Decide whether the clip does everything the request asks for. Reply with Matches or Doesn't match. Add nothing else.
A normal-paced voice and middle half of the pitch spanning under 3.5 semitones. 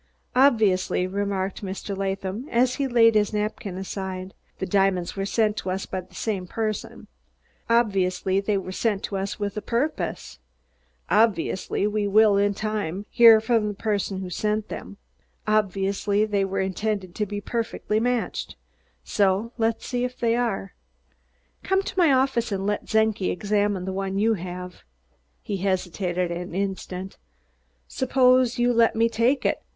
Matches